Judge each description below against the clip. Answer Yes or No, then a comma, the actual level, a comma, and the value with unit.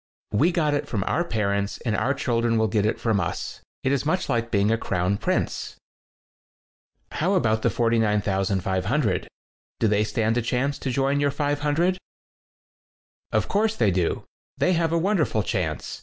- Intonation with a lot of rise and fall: Yes, wide, 5.9 semitones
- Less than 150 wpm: No, average, 160 wpm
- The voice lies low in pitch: Yes, low, 115 Hz